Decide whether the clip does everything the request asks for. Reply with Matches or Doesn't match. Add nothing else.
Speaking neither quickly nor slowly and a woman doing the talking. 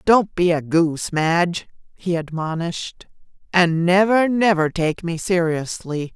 Doesn't match